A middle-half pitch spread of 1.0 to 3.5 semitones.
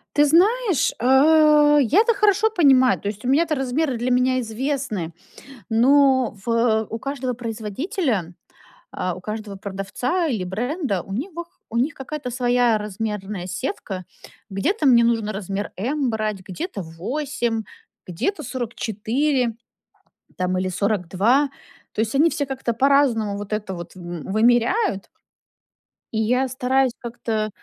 No: average, 5.0 semitones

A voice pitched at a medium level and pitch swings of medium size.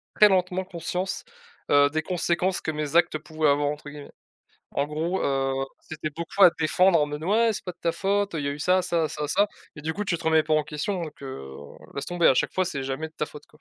Yes: medium, 160 Hz; average, 3.6 semitones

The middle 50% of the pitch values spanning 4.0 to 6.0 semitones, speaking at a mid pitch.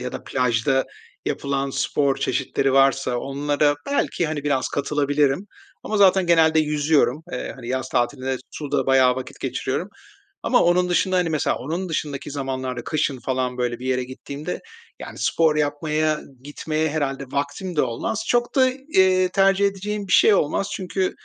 Yes: average, 5.0 semitones; medium, 145 Hz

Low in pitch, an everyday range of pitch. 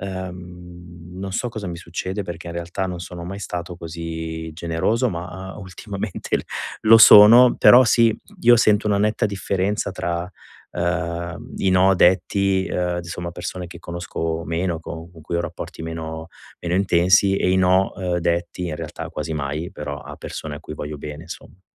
No: very low, 90 Hz; narrow, 2.3 semitones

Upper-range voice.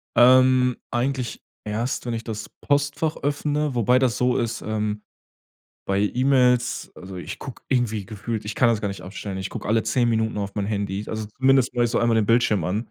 No: low, 115 Hz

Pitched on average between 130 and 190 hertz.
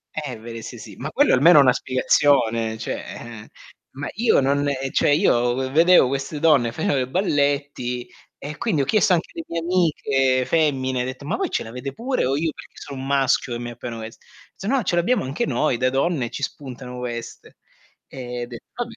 Yes: low, 135 Hz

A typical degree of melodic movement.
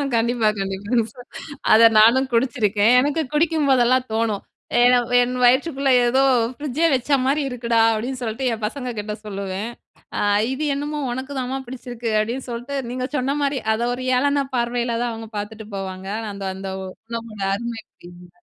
Yes: average, 3.2 semitones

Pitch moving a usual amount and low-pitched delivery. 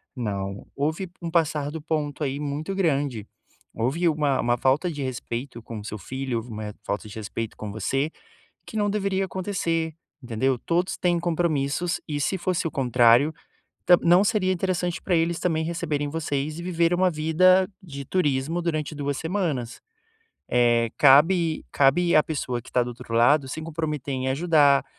No: average, 4.7 semitones; medium, 150 Hz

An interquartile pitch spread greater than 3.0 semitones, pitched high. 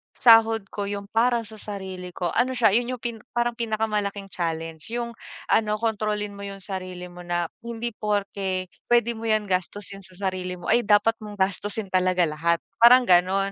Yes: average, 3.4 semitones; high, 205 Hz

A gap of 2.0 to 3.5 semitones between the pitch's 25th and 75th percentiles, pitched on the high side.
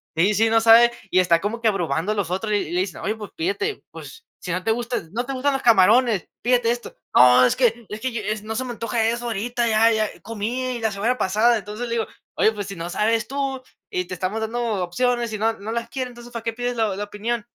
Yes: average, 2.8 semitones; high, 225 Hz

